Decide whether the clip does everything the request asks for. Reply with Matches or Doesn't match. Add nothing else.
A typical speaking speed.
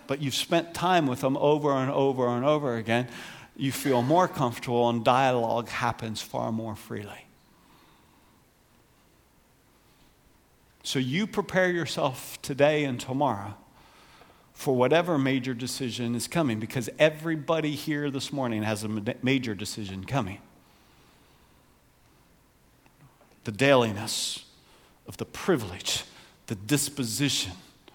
Doesn't match